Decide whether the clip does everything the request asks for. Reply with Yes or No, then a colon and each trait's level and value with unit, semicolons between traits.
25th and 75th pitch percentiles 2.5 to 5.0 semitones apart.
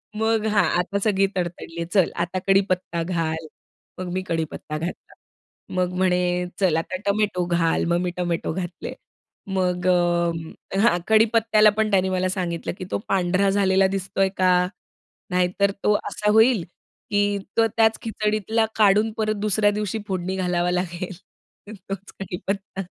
Yes: average, 2.8 semitones